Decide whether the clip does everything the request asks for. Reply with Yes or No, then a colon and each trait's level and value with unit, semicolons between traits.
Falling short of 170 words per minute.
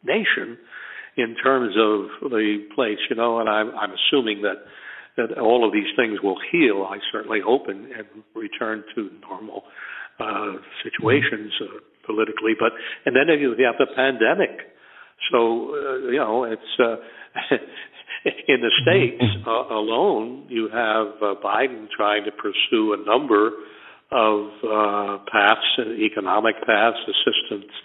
Yes: average, 140 wpm